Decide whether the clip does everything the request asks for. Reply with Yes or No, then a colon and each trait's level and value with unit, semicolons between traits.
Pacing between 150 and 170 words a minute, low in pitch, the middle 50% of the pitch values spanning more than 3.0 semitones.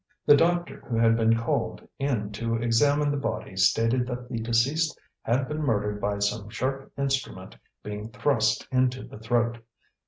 Yes: average, 160 wpm; low, 115 Hz; average, 3.4 semitones